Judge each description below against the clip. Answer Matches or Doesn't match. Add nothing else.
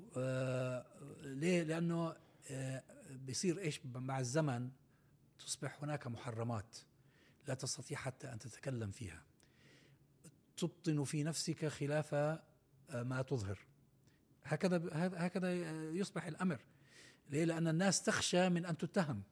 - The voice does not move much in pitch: Doesn't match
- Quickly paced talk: Doesn't match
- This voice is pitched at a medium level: Matches